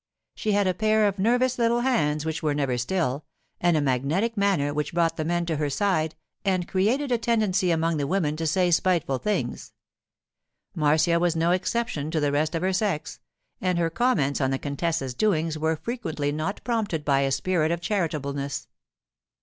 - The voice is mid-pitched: Yes, medium, 165 Hz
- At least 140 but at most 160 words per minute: No, average, 185 wpm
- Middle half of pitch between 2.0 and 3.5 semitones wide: No, average, 5.0 semitones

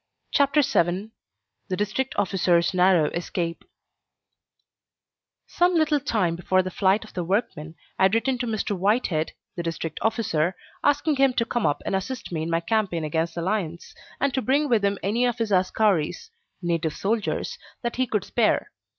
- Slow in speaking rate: No, average, 170 wpm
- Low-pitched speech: No, high, 200 Hz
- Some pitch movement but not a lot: No, wide, 5.8 semitones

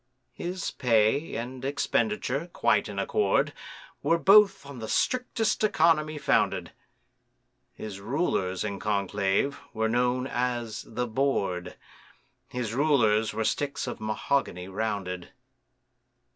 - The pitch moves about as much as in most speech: No, wide, 6.1 semitones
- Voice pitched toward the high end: No, low, 125 Hz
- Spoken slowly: Yes, slow, 110 wpm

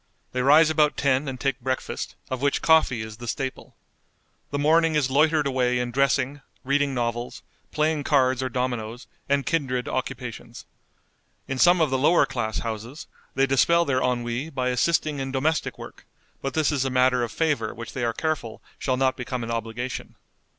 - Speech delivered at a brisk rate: No, average, 180 wpm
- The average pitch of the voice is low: Yes, low, 130 Hz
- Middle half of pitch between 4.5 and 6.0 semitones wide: No, average, 2.8 semitones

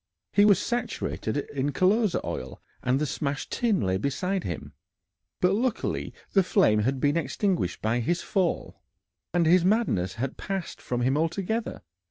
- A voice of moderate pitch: Yes, medium, 170 Hz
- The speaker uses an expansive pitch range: Yes, wide, 7.3 semitones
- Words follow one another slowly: No, average, 155 wpm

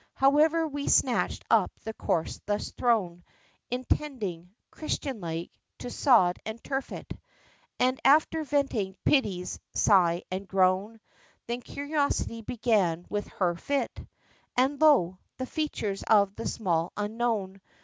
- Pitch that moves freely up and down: Yes, wide, 6.4 semitones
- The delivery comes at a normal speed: No, slow, 125 wpm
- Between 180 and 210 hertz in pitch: No, high, 220 Hz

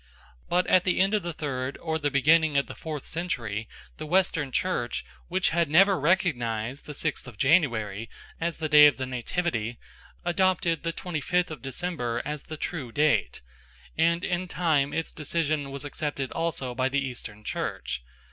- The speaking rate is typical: Yes, average, 175 wpm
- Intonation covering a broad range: No, average, 4.5 semitones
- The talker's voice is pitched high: No, medium, 150 Hz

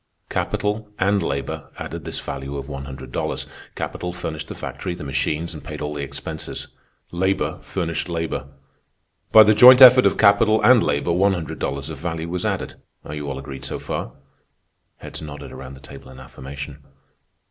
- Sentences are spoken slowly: No, average, 180 wpm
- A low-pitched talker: Yes, very low, 75 Hz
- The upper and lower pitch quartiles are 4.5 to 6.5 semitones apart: Yes, wide, 5.4 semitones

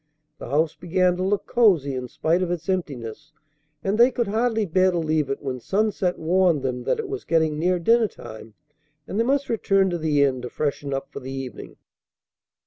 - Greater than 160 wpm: Yes, fast, 205 wpm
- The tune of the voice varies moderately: No, wide, 5.9 semitones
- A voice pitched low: No, medium, 170 Hz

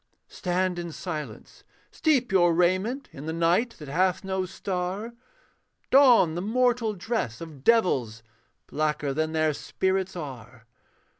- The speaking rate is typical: No, slow, 130 wpm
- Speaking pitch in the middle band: Yes, medium, 180 Hz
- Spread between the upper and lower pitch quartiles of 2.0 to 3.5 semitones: No, average, 4.9 semitones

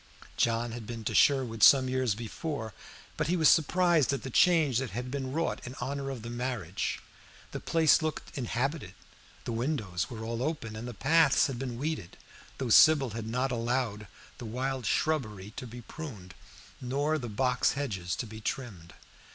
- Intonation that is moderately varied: Yes, average, 3.9 semitones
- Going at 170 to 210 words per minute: Yes, average, 175 wpm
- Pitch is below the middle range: Yes, low, 125 Hz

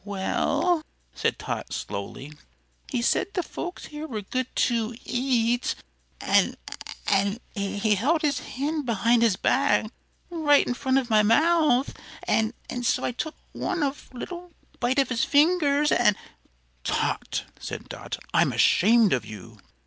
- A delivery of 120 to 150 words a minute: Yes, average, 145 wpm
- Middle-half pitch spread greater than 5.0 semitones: Yes, wide, 5.6 semitones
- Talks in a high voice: Yes, high, 245 Hz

